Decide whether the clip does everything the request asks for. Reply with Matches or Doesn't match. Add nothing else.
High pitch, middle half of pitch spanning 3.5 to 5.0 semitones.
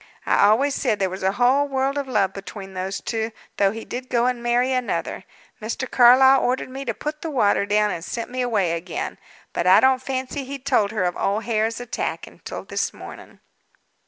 Matches